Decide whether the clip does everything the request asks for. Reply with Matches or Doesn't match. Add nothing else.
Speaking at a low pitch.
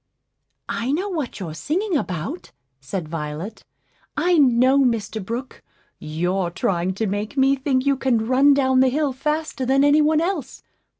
Doesn't match